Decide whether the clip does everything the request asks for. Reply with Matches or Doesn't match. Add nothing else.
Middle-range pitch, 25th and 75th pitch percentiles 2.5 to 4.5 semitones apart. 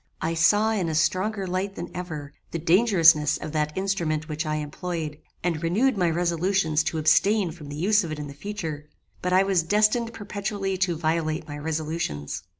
Matches